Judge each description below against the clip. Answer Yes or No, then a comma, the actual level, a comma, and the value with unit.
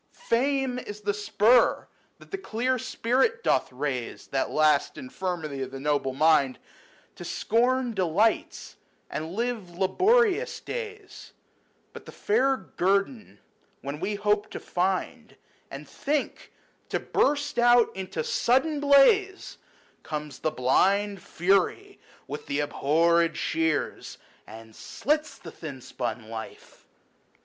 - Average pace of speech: No, slow, 120 wpm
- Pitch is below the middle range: No, high, 200 Hz